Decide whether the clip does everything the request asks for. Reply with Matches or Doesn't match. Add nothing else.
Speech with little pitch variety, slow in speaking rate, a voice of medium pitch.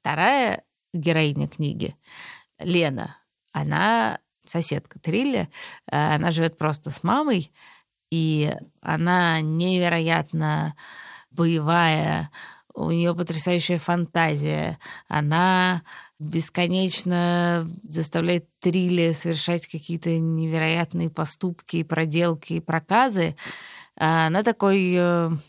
Matches